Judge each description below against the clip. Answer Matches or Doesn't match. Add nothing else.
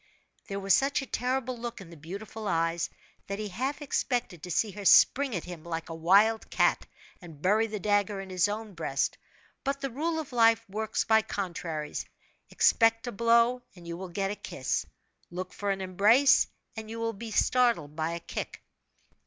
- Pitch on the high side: Matches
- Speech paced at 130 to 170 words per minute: Doesn't match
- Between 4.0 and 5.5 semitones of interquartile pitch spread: Matches